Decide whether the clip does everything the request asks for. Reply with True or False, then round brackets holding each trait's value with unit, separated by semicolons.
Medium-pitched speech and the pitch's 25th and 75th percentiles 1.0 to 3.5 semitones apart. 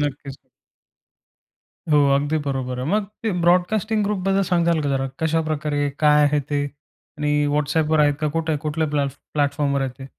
True (150 Hz; 2.4 semitones)